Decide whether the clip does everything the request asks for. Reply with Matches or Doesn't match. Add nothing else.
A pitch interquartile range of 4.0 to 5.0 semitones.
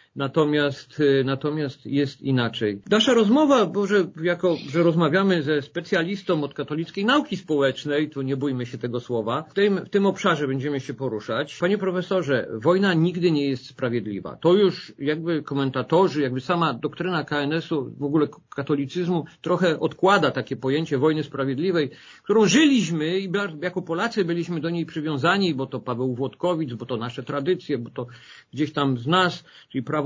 Matches